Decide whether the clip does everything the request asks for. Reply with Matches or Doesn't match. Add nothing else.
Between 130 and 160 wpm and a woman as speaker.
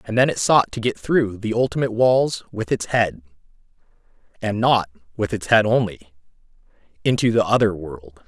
Doesn't match